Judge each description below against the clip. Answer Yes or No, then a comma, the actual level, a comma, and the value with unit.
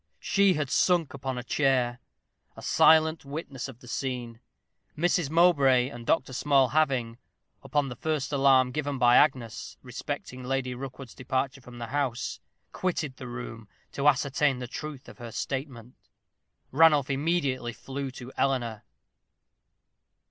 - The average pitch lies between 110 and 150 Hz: Yes, low, 135 Hz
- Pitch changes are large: No, average, 2.8 semitones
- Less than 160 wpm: Yes, average, 140 wpm